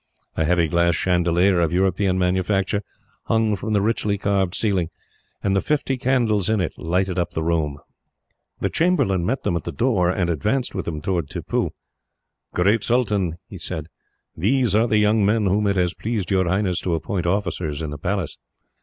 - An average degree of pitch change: Yes, average, 3.5 semitones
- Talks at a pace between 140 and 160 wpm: No, average, 180 wpm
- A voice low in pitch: Yes, very low, 95 Hz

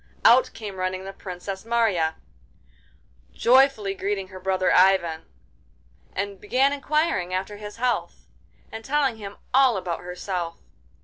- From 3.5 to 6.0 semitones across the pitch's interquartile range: Yes, average, 4.2 semitones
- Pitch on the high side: Yes, high, 200 Hz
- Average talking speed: No, slow, 125 wpm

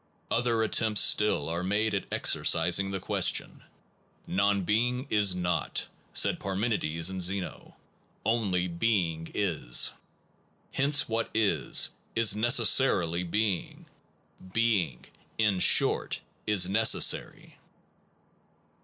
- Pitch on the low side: Yes, low, 100 Hz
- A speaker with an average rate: No, slow, 105 wpm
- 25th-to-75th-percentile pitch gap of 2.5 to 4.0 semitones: Yes, average, 3.7 semitones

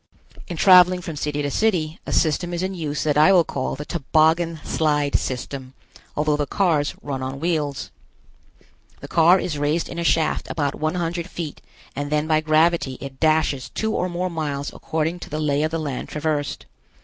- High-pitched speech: No, medium, 155 Hz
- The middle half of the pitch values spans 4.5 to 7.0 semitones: No, average, 2.8 semitones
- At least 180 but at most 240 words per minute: Yes, average, 190 wpm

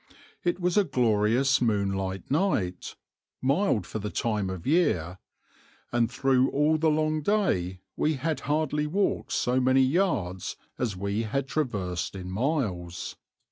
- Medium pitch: No, low, 125 Hz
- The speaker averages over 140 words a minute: No, slow, 135 wpm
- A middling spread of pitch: No, wide, 7.9 semitones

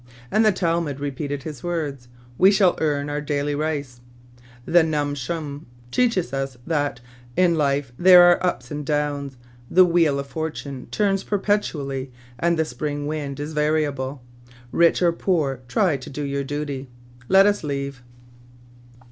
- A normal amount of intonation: Yes, average, 3.5 semitones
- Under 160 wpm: No, average, 165 wpm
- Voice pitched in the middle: Yes, medium, 145 Hz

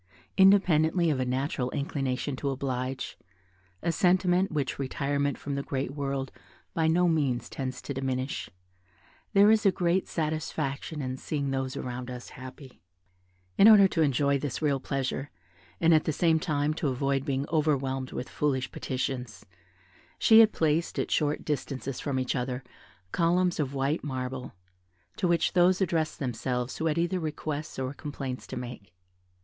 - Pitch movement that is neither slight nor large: Yes, average, 3.6 semitones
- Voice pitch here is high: No, medium, 140 Hz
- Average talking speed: Yes, average, 155 wpm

